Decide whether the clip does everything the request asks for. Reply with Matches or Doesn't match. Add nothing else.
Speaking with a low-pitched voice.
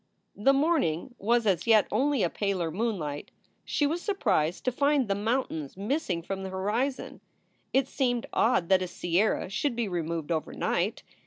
Doesn't match